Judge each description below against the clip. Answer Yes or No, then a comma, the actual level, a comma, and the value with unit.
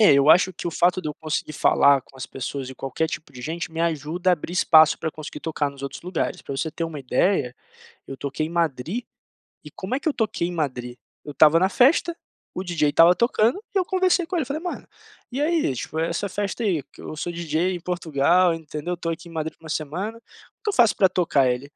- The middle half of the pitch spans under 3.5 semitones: No, average, 4.2 semitones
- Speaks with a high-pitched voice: No, medium, 165 Hz